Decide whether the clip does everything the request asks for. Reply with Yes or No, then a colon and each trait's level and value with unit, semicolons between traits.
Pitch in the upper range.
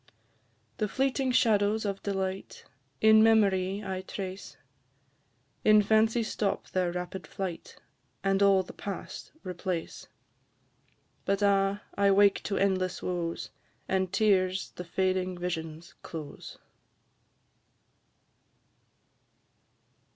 Yes: high, 195 Hz